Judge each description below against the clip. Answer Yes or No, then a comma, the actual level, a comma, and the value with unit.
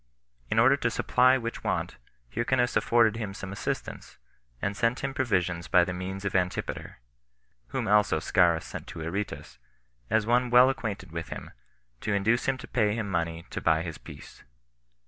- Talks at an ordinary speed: Yes, average, 170 wpm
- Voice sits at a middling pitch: No, low, 100 Hz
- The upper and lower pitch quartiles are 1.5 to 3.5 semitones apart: No, average, 4.9 semitones